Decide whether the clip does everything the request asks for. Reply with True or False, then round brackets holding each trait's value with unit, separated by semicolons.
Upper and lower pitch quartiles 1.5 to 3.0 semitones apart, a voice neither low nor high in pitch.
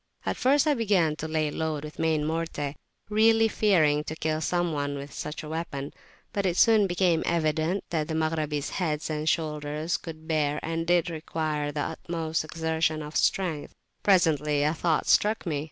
True (2.4 semitones; 160 Hz)